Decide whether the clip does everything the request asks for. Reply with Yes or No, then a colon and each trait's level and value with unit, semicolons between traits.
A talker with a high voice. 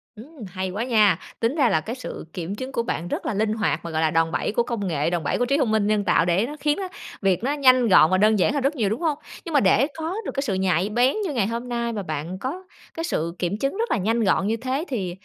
Yes: high, 220 Hz